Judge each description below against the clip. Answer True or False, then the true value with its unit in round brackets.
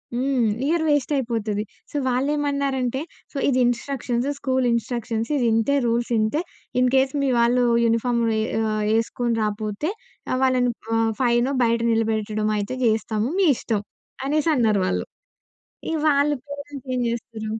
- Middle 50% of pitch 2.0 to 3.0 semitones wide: False (3.4 semitones)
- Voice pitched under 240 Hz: False (245 Hz)